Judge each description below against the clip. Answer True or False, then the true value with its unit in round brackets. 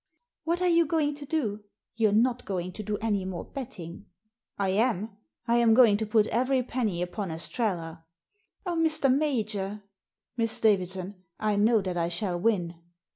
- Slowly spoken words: False (175 wpm)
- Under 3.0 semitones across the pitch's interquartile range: False (4.9 semitones)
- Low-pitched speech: False (215 Hz)